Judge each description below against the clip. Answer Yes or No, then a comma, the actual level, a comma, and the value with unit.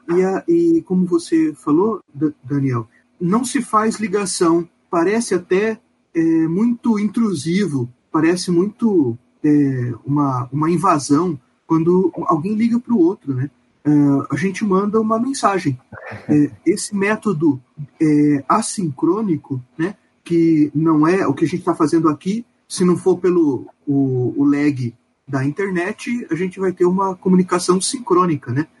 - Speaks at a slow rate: No, average, 140 wpm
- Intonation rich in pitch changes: Yes, wide, 6.1 semitones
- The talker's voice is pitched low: No, medium, 175 Hz